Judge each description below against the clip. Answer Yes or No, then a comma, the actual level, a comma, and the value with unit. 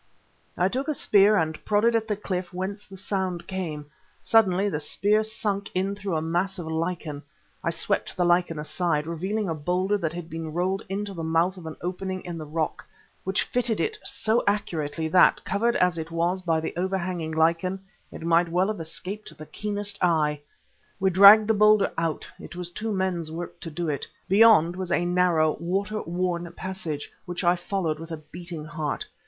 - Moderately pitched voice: Yes, medium, 180 Hz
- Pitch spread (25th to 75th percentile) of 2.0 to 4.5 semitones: Yes, average, 3.2 semitones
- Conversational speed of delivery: Yes, average, 190 wpm